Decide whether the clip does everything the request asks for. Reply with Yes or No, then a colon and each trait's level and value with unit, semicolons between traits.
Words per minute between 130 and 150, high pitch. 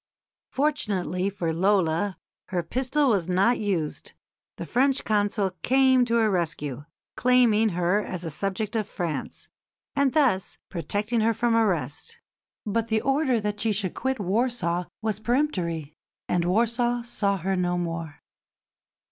Yes: average, 140 wpm; high, 205 Hz